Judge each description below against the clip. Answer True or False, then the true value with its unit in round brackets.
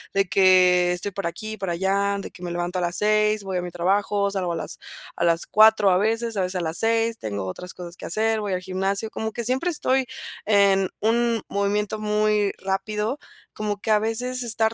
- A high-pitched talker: True (200 Hz)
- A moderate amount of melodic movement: True (3.1 semitones)